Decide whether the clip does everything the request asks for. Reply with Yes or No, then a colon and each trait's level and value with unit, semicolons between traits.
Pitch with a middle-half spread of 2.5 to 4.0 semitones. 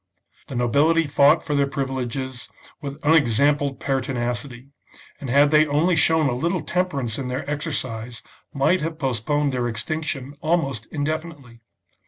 Yes: average, 3.6 semitones